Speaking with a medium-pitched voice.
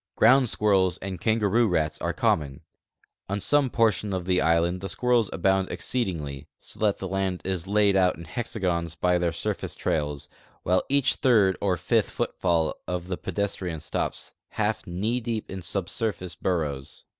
No: very low, 95 Hz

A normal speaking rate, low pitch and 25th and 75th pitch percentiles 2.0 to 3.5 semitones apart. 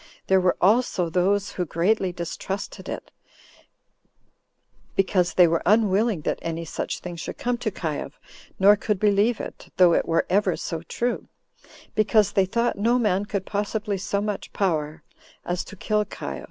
No: average, 160 wpm; high, 195 Hz; average, 3.1 semitones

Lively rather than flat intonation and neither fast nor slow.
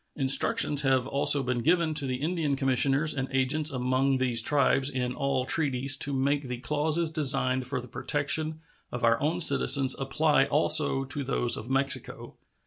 No: narrow, 2.4 semitones; average, 165 wpm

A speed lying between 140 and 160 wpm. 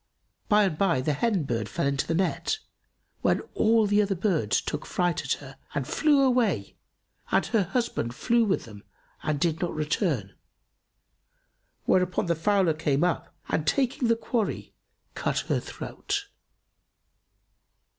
Yes: average, 145 wpm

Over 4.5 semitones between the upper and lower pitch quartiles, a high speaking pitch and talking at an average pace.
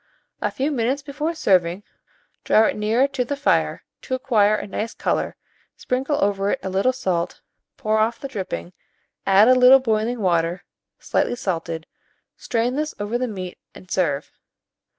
Yes: average, 5.3 semitones; high, 220 Hz; average, 160 wpm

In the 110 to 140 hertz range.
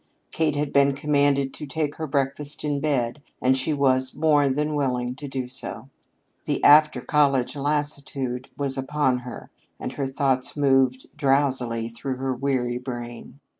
Yes: low, 135 Hz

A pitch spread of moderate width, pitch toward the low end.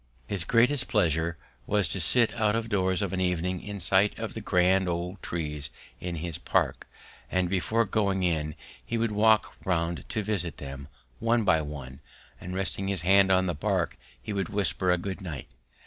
Yes: average, 3.3 semitones; very low, 95 Hz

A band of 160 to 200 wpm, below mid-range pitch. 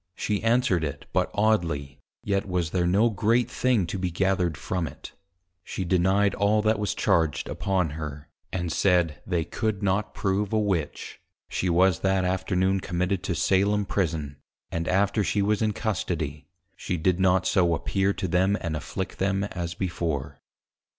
Yes: average, 170 wpm; very low, 95 Hz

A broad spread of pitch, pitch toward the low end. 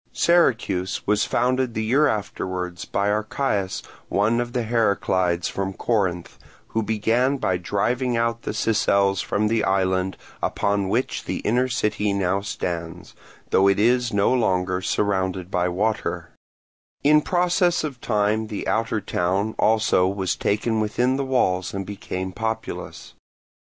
No: average, 3.8 semitones; low, 105 Hz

